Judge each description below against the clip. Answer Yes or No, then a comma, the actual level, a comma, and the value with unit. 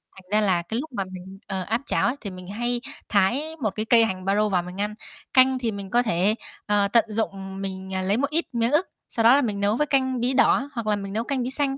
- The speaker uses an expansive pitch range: No, average, 4.1 semitones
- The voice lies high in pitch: Yes, high, 215 Hz